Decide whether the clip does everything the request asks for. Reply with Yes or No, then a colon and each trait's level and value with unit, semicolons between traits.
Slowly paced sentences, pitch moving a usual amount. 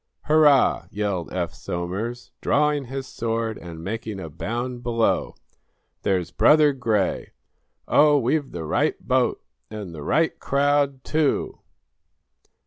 No: slow, 120 wpm; wide, 6.5 semitones